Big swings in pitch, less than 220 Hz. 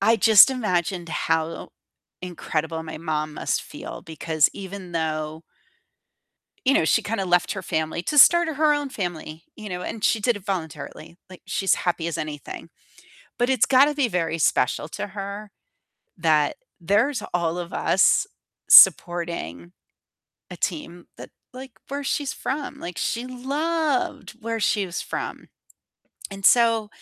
Yes: wide, 6.4 semitones; high, 190 Hz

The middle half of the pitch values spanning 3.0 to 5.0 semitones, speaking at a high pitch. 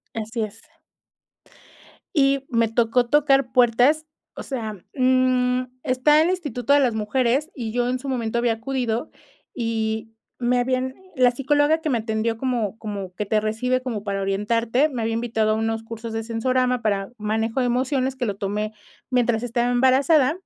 No: narrow, 2.6 semitones; high, 240 Hz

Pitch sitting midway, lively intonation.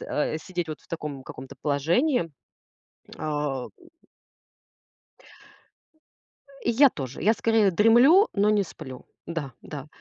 Yes: medium, 165 Hz; wide, 7.2 semitones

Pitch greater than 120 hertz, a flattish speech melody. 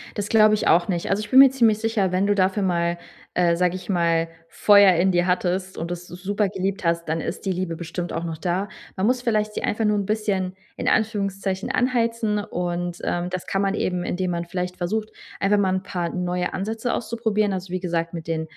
No: medium, 185 Hz; average, 3.0 semitones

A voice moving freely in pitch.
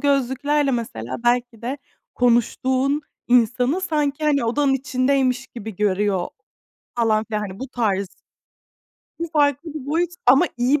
No: average, 3.8 semitones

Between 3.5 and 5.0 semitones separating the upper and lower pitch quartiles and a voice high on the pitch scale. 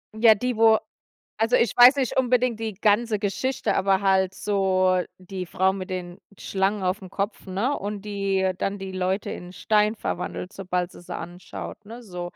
No: average, 2.8 semitones; high, 195 Hz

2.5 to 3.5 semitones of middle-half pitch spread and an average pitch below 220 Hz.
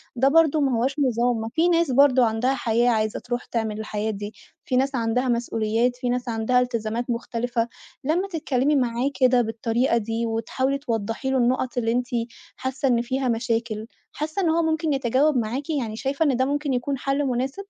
No: average, 3.1 semitones; very high, 250 Hz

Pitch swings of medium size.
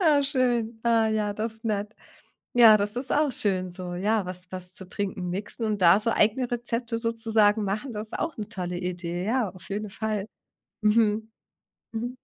Yes: average, 3.0 semitones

